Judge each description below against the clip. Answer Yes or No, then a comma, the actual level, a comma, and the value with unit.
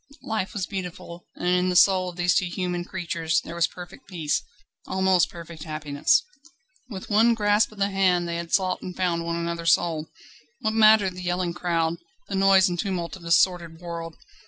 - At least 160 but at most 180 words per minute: No, average, 190 wpm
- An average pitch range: No, narrow, 2.0 semitones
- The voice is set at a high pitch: No, medium, 180 Hz